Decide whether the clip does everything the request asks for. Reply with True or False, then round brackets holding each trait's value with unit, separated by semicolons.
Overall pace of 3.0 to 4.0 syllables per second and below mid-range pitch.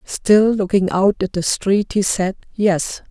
False (3.6 syllables/s; 195 Hz)